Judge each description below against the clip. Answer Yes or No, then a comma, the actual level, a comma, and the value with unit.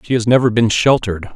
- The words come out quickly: Yes, fast, 220 wpm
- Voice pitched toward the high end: No, low, 115 Hz